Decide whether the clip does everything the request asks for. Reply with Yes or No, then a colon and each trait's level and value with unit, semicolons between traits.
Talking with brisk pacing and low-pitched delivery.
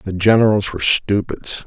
No: average, 145 wpm; low, 100 Hz